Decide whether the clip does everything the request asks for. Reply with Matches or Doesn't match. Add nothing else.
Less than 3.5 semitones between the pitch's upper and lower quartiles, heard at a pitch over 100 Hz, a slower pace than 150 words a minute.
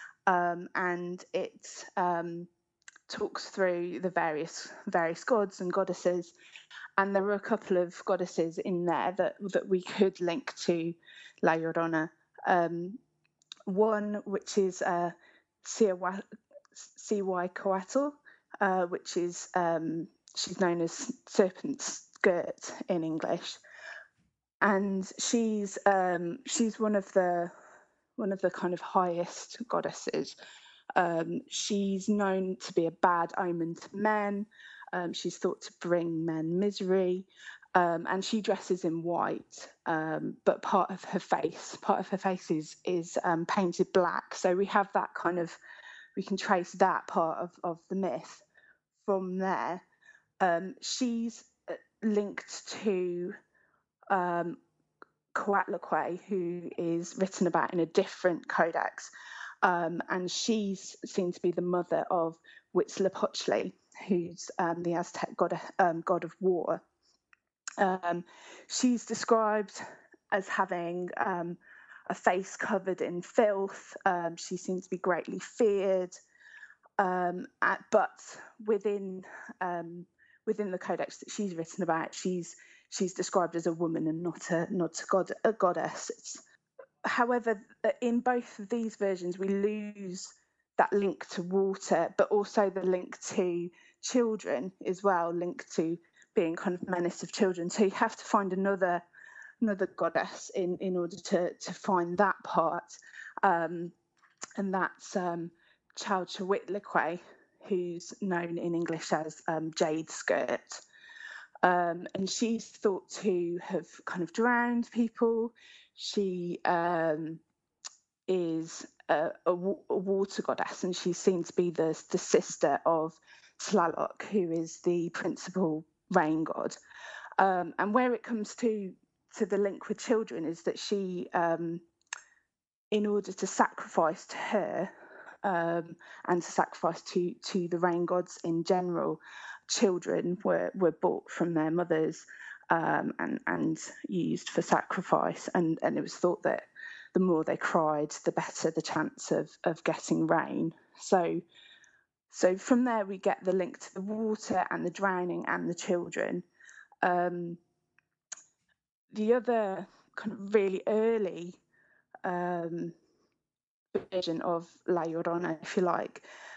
Matches